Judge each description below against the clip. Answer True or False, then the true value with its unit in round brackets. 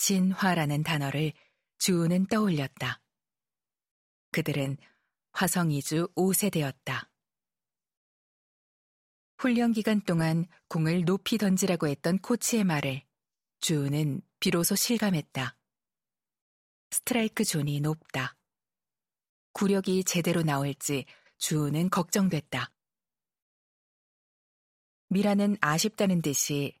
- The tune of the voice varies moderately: True (4.9 semitones)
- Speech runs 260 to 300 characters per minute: False (200 characters per minute)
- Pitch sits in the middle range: True (175 Hz)